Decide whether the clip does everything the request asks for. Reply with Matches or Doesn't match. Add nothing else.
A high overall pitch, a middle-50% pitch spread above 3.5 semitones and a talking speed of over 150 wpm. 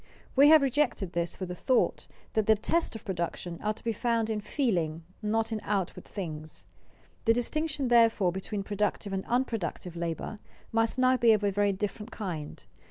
Matches